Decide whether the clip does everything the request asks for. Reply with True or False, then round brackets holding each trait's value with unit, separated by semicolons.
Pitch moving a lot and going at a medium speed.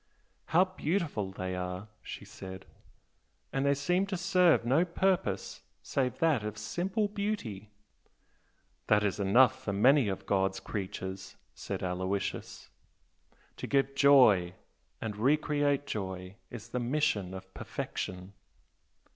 False (7.6 semitones; 125 wpm)